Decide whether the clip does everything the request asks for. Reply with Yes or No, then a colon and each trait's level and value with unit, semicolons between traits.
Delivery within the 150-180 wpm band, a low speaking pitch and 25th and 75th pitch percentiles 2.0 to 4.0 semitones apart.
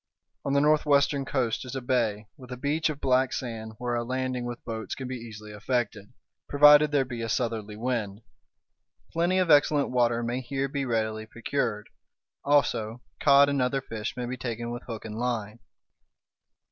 Yes: average, 175 wpm; low, 125 Hz; average, 3.4 semitones